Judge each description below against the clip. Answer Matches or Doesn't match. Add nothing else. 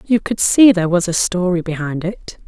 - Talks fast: Matches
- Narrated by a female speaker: Matches